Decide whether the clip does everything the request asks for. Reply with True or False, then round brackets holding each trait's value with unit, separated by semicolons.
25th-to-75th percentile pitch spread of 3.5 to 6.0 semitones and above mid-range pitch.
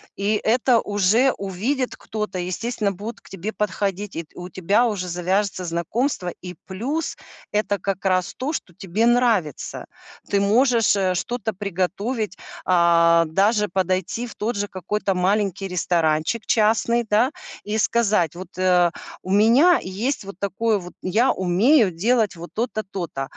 True (3.8 semitones; 200 Hz)